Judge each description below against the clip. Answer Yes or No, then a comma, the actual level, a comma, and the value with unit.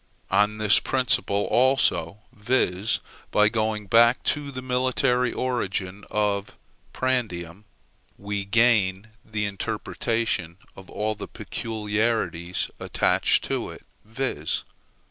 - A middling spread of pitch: Yes, average, 3.5 semitones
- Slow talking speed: Yes, slow, 105 wpm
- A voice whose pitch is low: Yes, low, 105 Hz